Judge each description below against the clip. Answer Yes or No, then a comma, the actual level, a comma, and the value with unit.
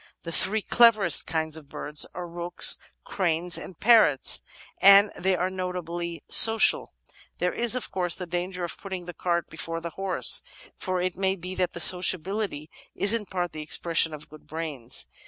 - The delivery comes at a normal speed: Yes, average, 175 wpm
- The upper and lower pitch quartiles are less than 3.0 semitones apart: Yes, narrow, 2.5 semitones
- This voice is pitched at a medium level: Yes, medium, 180 Hz